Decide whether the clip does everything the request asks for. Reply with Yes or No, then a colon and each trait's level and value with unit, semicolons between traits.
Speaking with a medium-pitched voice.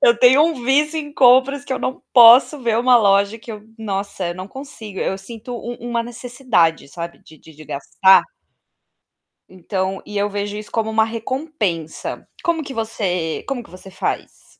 No: high, 225 Hz